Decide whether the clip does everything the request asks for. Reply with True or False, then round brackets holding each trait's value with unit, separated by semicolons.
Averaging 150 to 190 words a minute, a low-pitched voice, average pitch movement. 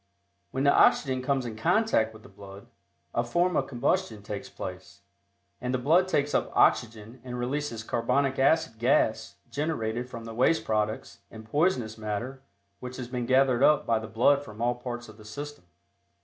True (175 wpm; 120 Hz; 3.7 semitones)